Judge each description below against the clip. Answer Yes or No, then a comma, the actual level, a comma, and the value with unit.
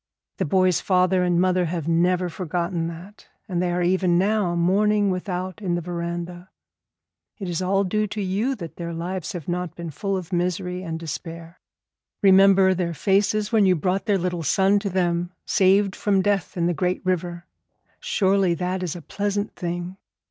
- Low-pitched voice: No, medium, 180 Hz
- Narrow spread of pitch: Yes, narrow, 2.0 semitones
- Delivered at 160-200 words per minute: Yes, average, 175 wpm